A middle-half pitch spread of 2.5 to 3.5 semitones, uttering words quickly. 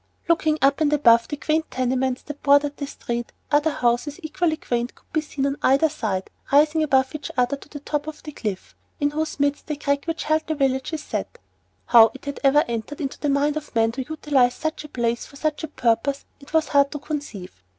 Yes: average, 2.9 semitones; fast, 220 wpm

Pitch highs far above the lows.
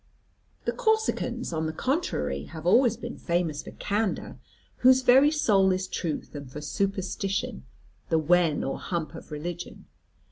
Yes: wide, 6.8 semitones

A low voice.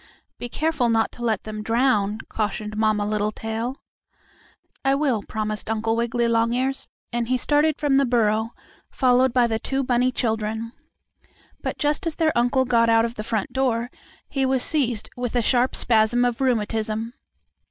No: high, 235 Hz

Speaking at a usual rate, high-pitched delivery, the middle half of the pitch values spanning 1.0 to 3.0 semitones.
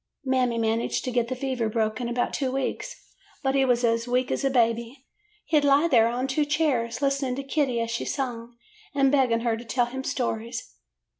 No: fast, 210 wpm; very high, 250 Hz; narrow, 2.5 semitones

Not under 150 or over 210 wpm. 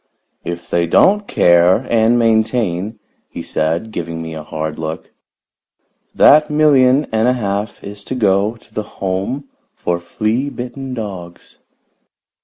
No: slow, 135 wpm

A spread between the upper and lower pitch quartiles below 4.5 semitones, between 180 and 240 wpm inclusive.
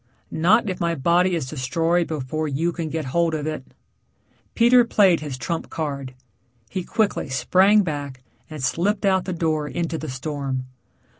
No: average, 4.0 semitones; average, 160 wpm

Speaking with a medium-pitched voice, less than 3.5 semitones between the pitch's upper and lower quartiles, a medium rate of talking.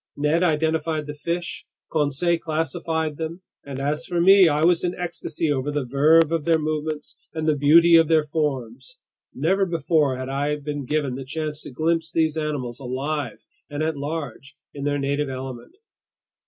Yes: medium, 150 Hz; narrow, 2.4 semitones; average, 170 wpm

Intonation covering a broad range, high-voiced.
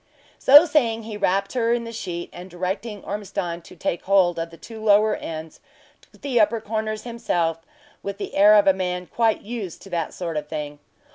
No: average, 4.3 semitones; high, 200 Hz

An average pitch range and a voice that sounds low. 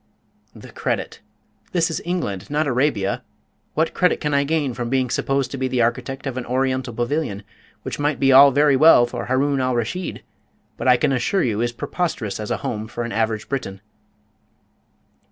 Yes: average, 3.2 semitones; low, 130 Hz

